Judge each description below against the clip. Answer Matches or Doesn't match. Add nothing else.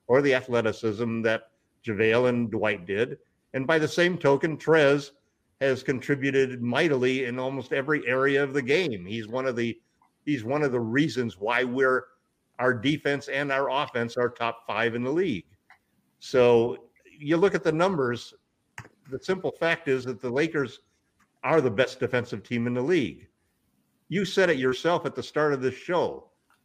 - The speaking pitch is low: Matches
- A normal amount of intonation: Matches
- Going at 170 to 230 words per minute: Matches